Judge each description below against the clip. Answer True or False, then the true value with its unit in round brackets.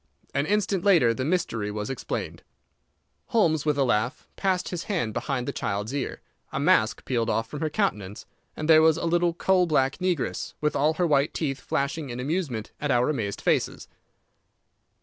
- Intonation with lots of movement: True (5.8 semitones)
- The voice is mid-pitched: True (150 Hz)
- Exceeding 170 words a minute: True (180 wpm)